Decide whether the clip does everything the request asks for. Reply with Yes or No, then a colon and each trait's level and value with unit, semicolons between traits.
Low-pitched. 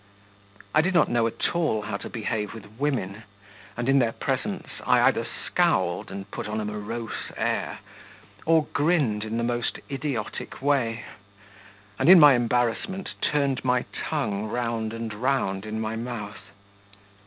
Yes: low, 115 Hz